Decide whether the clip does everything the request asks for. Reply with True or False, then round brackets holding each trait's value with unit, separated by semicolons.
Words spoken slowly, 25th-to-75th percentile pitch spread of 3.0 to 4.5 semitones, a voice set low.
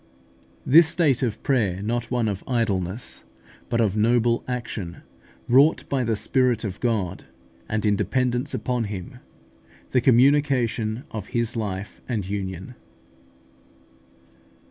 True (120 wpm; 3.5 semitones; 115 Hz)